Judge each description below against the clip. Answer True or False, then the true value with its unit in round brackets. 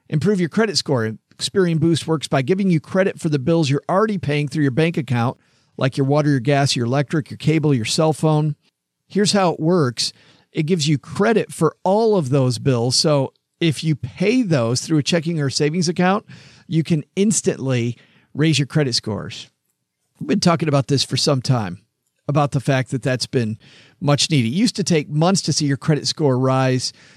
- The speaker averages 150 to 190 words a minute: False (200 wpm)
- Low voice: False (150 Hz)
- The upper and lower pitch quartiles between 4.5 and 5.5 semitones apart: False (3.7 semitones)